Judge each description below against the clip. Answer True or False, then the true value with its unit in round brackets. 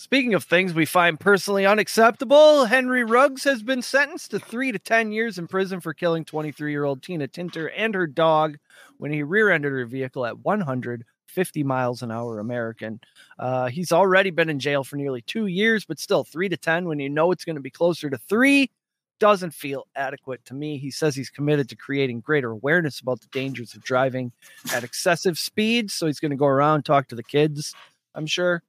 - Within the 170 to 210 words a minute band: True (200 wpm)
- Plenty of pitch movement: True (6.1 semitones)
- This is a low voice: False (155 Hz)